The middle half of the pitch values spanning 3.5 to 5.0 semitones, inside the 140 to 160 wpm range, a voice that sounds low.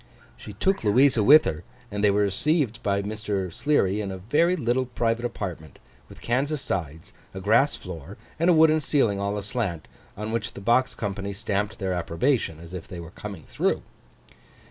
No: average, 4.7 semitones; average, 180 wpm; low, 105 Hz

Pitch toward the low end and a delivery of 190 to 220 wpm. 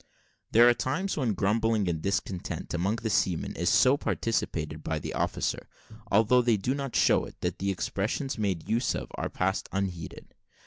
No: low, 105 Hz; average, 175 wpm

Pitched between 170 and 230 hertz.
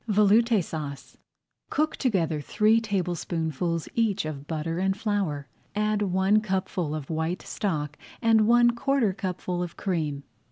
Yes: high, 190 Hz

